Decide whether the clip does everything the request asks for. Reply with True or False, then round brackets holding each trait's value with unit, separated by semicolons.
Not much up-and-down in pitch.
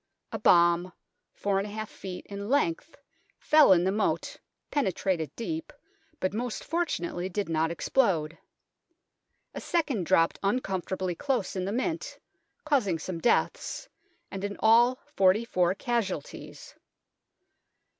False (5.3 semitones)